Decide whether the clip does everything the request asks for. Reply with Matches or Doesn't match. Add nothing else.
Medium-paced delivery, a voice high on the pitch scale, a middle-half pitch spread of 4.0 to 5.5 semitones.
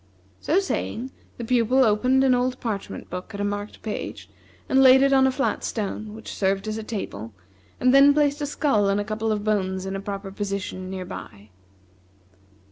Matches